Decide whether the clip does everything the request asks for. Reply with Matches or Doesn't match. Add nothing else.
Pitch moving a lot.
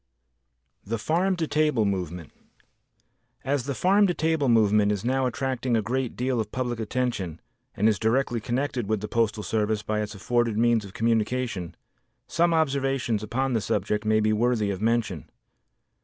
Doesn't match